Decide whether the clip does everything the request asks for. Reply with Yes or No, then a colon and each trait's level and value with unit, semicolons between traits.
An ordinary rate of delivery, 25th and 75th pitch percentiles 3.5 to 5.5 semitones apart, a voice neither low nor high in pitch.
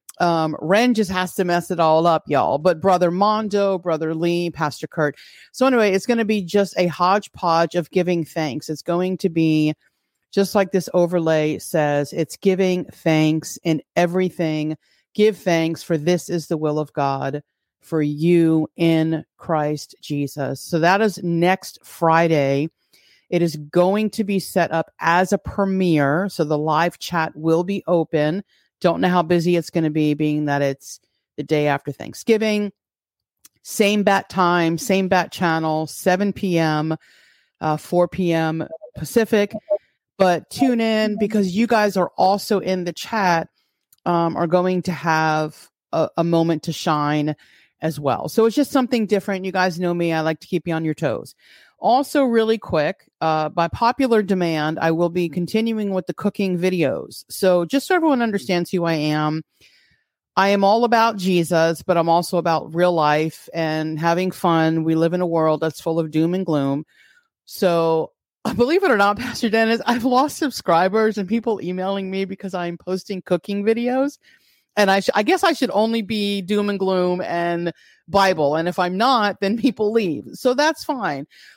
Yes: average, 175 wpm; average, 4.0 semitones; medium, 175 Hz